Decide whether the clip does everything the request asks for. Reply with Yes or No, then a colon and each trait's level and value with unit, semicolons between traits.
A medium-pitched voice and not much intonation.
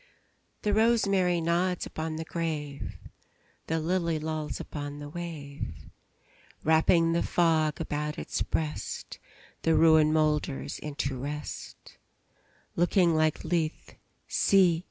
Yes: medium, 160 Hz; narrow, 2.1 semitones